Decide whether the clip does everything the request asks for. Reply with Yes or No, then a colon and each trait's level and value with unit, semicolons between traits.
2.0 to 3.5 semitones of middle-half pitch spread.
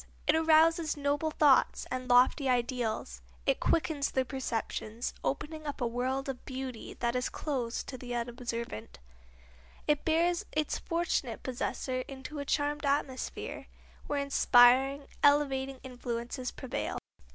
Yes: average, 3.0 semitones